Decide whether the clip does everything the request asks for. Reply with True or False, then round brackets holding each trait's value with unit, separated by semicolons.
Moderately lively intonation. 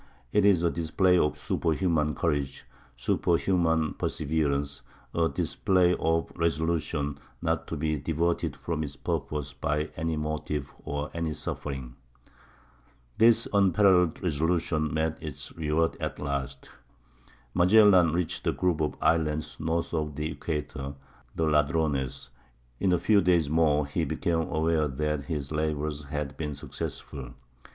False (2.3 semitones)